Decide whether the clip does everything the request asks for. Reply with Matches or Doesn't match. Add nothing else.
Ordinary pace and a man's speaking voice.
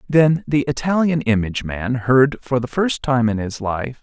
Matches